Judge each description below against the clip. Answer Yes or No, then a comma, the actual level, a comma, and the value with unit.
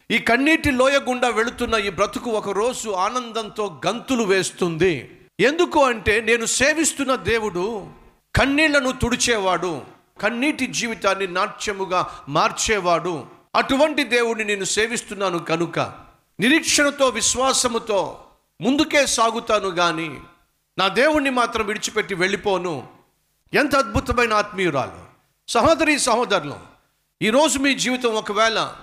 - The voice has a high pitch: Yes, high, 225 Hz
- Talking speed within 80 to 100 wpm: Yes, average, 95 wpm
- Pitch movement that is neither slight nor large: Yes, average, 4.9 semitones